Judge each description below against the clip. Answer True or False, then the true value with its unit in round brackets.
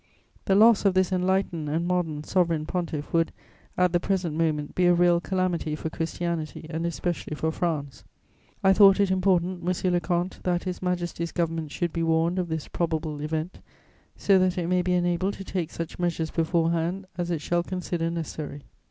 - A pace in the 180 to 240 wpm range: True (185 wpm)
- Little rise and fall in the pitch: True (2.0 semitones)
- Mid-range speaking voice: True (175 Hz)